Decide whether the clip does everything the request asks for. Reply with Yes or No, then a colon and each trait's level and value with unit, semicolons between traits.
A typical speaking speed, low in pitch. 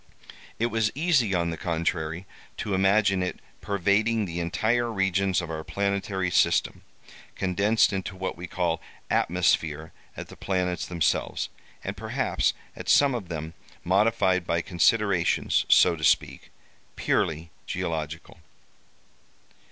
No: slow, 125 wpm; very low, 95 Hz